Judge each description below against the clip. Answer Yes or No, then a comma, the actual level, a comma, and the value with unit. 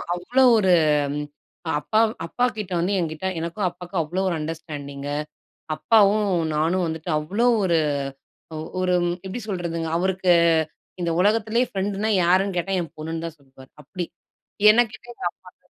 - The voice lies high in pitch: No, medium, 180 Hz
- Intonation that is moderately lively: Yes, average, 3.6 semitones